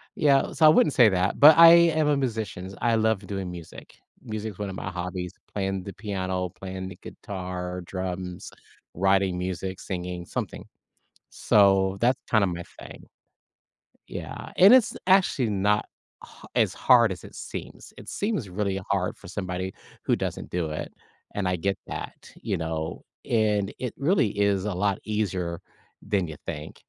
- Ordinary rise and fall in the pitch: Yes, average, 3.4 semitones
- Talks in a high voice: No, very low, 95 Hz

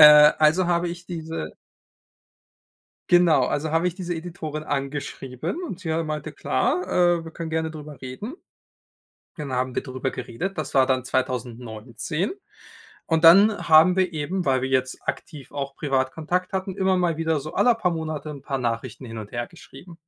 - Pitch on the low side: No, medium, 155 Hz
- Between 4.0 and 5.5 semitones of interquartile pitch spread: Yes, average, 4.7 semitones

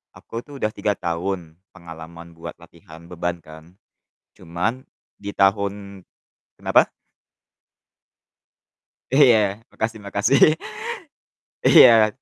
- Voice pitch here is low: Yes, very low, 95 Hz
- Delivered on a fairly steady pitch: No, average, 4.2 semitones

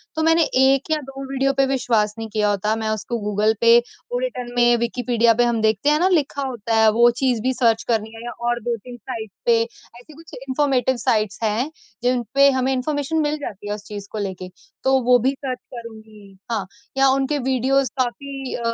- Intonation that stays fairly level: No, average, 3.5 semitones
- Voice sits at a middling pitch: No, high, 240 Hz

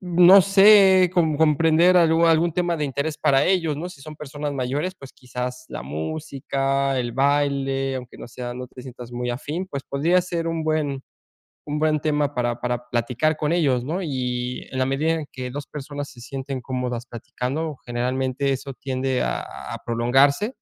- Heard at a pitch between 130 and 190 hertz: Yes, medium, 140 Hz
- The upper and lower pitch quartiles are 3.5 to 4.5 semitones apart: Yes, average, 4.0 semitones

